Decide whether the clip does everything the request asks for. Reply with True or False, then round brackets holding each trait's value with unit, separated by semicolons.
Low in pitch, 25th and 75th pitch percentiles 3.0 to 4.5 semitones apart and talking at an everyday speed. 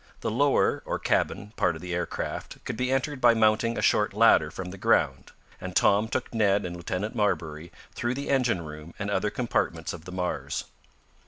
False (100 Hz; 5.1 semitones; 190 wpm)